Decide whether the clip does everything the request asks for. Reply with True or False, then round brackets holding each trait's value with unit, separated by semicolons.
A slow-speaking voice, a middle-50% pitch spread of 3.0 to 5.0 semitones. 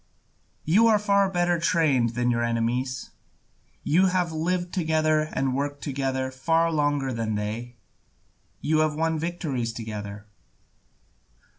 False (125 wpm; 5.4 semitones)